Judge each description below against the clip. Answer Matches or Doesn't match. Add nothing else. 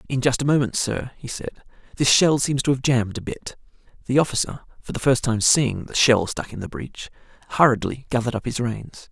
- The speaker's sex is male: Matches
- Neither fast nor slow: Doesn't match